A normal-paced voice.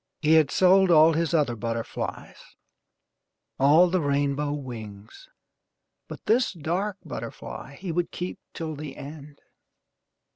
No: slow, 120 wpm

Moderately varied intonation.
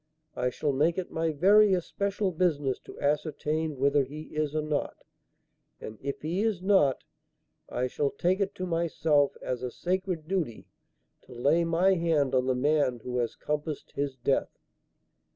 Yes: average, 4.1 semitones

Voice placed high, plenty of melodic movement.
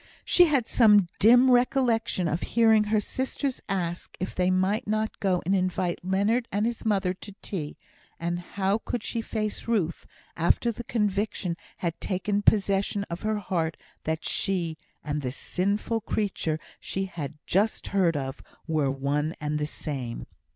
No: high, 195 Hz; average, 4.3 semitones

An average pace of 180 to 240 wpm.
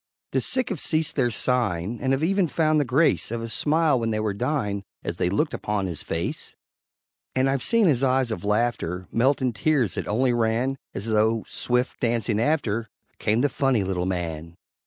Yes: average, 195 wpm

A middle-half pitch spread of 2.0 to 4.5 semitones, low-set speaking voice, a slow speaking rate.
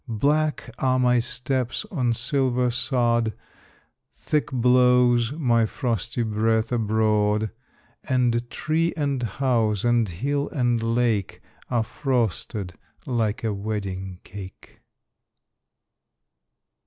Yes: narrow, 2.6 semitones; low, 120 Hz; slow, 95 wpm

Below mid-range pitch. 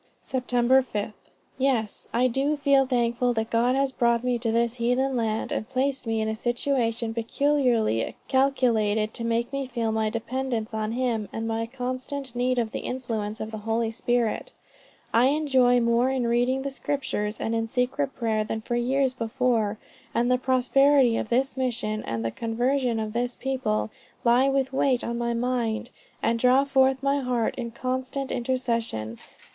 No: high, 245 Hz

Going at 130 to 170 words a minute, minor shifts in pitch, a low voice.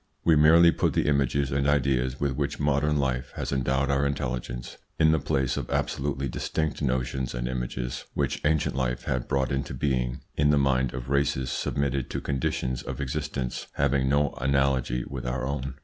No: average, 180 wpm; narrow, 2.0 semitones; very low, 70 Hz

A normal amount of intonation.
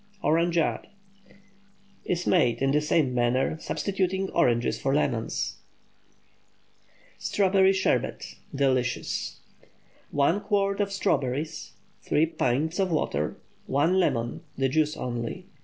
No: wide, 6.5 semitones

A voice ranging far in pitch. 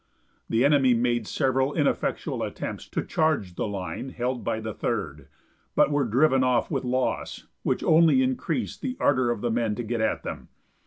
No: average, 3.0 semitones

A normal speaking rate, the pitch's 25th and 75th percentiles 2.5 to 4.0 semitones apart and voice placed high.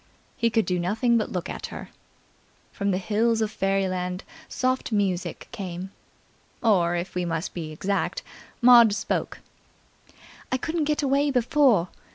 No: average, 145 wpm; average, 5.0 semitones; high, 205 Hz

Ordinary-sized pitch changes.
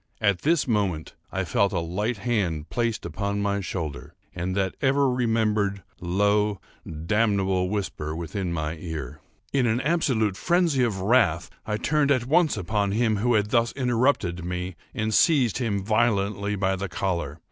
Yes: average, 4.3 semitones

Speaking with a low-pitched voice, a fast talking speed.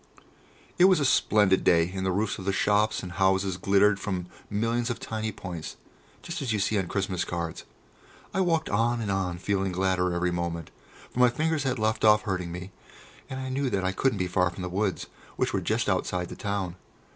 Yes: low, 100 Hz; fast, 210 wpm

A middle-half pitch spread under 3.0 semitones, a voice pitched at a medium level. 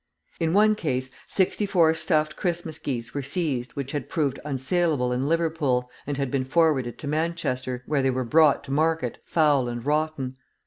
No: average, 3.8 semitones; medium, 145 Hz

